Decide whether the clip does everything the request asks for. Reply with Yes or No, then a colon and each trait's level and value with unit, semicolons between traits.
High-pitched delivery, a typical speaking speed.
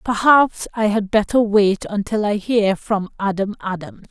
Yes: high, 205 Hz; average, 160 wpm